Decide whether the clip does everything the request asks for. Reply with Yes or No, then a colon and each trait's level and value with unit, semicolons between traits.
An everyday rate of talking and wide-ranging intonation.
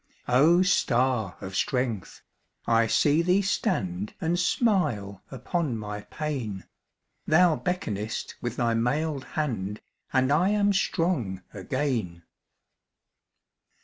No: slow, 105 wpm; wide, 7.9 semitones